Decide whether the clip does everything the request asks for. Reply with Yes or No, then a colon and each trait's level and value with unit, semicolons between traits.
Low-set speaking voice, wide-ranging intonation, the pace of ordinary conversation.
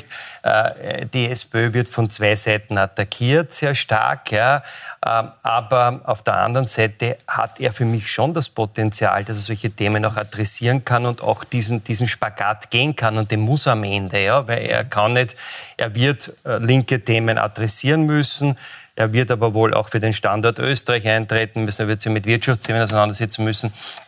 No: low, 115 Hz; narrow, 2.4 semitones; average, 175 wpm